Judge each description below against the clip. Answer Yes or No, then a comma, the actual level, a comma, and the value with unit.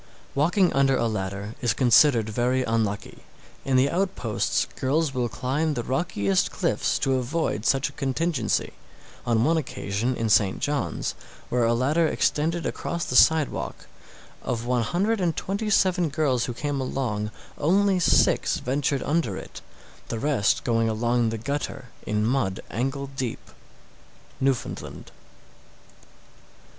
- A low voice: Yes, low, 130 Hz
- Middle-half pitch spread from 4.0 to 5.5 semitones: Yes, average, 4.7 semitones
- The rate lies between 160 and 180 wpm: No, average, 140 wpm